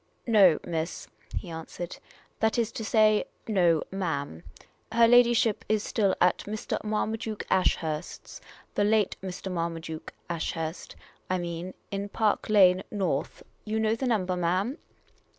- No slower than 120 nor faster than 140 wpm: No, average, 150 wpm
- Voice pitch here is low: No, high, 190 Hz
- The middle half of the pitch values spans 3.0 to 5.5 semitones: Yes, average, 4.1 semitones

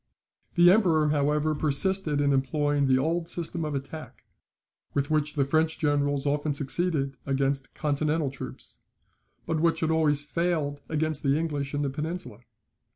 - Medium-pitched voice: Yes, medium, 150 Hz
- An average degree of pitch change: No, narrow, 2.2 semitones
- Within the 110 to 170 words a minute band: Yes, average, 150 wpm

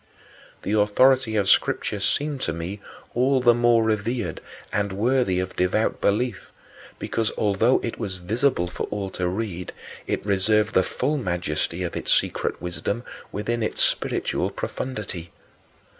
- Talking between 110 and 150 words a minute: Yes, average, 145 wpm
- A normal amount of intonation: Yes, average, 4.4 semitones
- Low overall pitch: Yes, low, 105 Hz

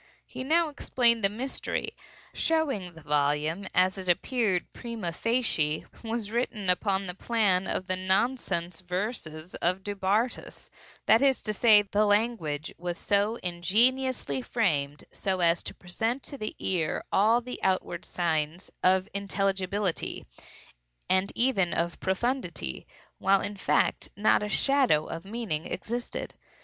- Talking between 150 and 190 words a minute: No, slow, 135 wpm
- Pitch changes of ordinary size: Yes, average, 4.8 semitones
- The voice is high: Yes, high, 195 Hz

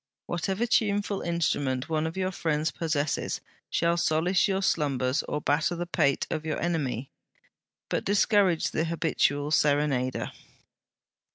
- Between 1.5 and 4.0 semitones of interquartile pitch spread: Yes, average, 3.3 semitones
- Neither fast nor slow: No, slow, 125 wpm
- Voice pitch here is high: No, medium, 160 Hz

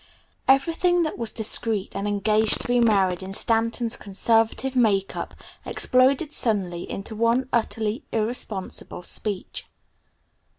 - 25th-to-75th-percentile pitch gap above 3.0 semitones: Yes, average, 3.4 semitones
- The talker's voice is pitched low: No, high, 225 Hz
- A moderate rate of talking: No, slow, 125 wpm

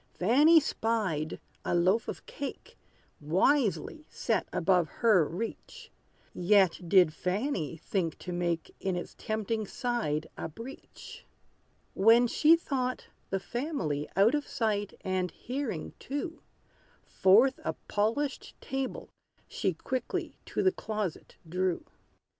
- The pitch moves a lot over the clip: Yes, wide, 6.3 semitones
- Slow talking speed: Yes, slow, 120 wpm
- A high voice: Yes, high, 210 Hz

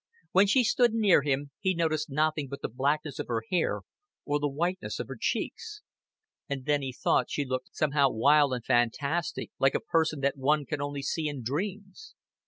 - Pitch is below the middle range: No, medium, 150 Hz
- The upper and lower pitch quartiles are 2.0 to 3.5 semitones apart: No, average, 3.9 semitones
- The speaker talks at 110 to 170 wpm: No, average, 190 wpm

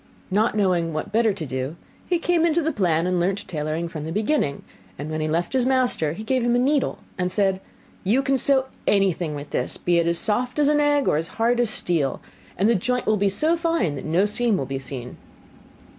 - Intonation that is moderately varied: No, wide, 7.5 semitones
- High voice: Yes, high, 200 Hz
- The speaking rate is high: Yes, fast, 230 wpm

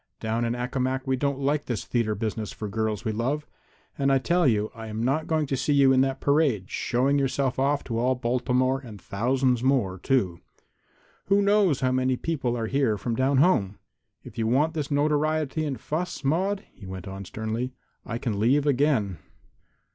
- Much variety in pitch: No, average, 4.1 semitones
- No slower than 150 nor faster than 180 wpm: No, average, 190 wpm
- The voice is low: Yes, low, 130 Hz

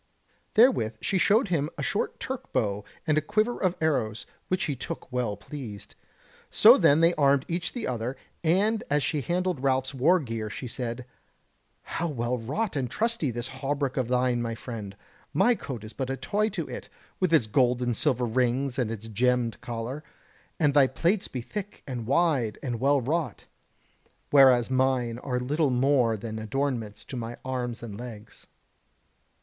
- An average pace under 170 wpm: No, average, 175 wpm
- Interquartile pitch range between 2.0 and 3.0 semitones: No, average, 4.5 semitones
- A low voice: Yes, low, 130 Hz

